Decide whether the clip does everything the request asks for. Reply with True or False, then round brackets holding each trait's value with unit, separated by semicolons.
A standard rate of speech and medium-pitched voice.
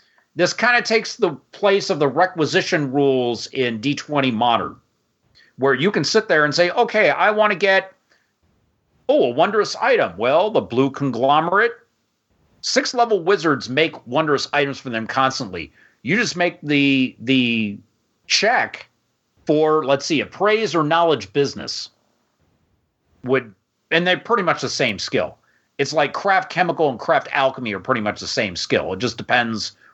True (160 wpm; 150 Hz)